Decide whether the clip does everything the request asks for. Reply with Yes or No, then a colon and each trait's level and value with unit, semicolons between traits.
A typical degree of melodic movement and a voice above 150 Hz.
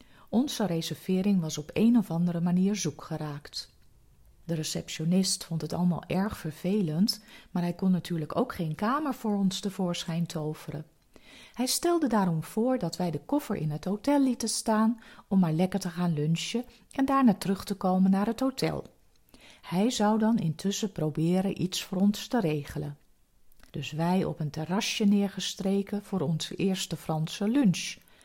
Yes: average, 4.3 semitones; high, 190 Hz